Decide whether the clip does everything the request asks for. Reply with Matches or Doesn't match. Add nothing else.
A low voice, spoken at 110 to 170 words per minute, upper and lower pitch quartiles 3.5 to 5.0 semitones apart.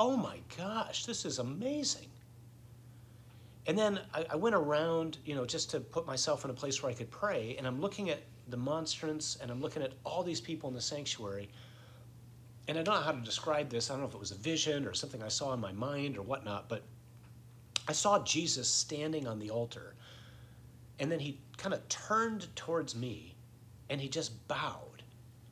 Doesn't match